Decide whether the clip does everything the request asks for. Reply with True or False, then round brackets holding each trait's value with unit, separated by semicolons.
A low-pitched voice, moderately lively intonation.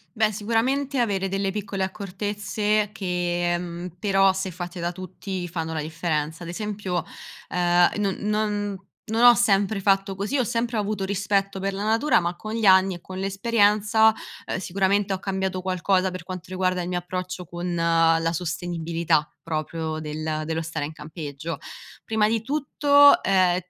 False (190 Hz; 3.0 semitones)